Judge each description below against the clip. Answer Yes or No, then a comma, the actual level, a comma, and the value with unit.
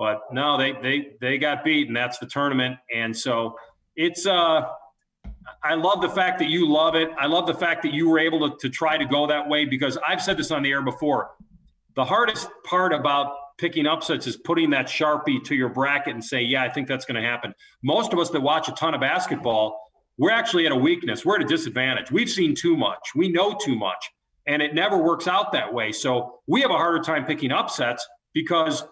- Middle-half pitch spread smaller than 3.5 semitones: No, average, 4.2 semitones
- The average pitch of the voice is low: No, medium, 150 Hz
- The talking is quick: Yes, fast, 230 wpm